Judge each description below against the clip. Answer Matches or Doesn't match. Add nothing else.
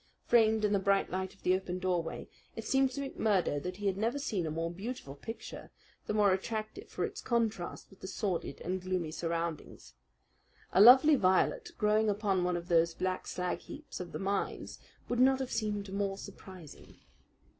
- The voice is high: Matches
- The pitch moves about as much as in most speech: Matches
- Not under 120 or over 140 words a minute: Doesn't match